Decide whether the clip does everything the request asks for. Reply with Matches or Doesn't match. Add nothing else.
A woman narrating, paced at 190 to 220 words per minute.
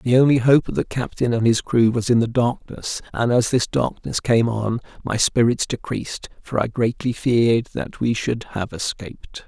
Doesn't match